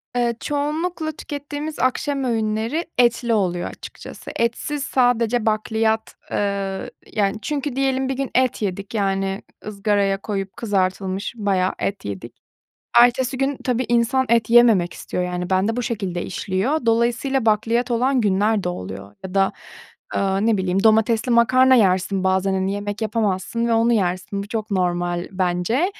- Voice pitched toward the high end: Yes, high, 220 Hz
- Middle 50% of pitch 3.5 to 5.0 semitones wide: Yes, average, 4.2 semitones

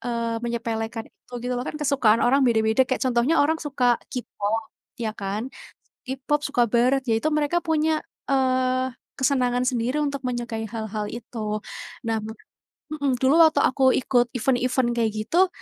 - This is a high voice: Yes, very high, 250 Hz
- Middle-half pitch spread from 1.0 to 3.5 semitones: Yes, average, 3.0 semitones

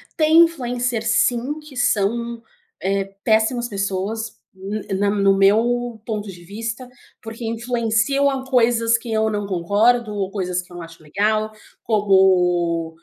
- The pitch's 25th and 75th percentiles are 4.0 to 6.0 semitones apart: No, average, 3.4 semitones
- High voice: Yes, high, 220 Hz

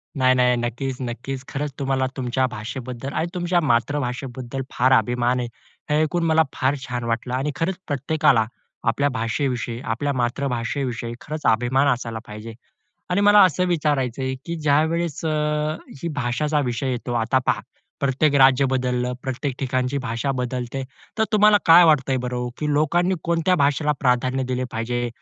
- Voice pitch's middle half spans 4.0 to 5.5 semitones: No, average, 3.4 semitones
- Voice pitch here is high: No, low, 130 Hz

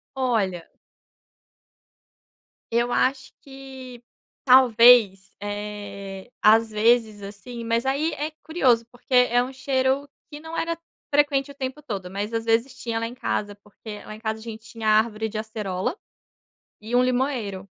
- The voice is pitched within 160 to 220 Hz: No, high, 230 Hz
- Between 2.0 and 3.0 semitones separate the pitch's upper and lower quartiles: No, average, 3.6 semitones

